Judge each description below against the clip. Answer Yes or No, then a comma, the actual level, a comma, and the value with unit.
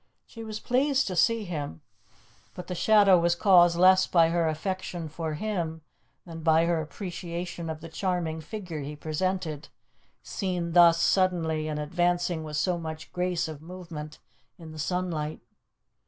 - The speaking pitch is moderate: Yes, medium, 170 Hz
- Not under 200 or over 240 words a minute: No, average, 155 wpm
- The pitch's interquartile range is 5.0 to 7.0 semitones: No, narrow, 2.5 semitones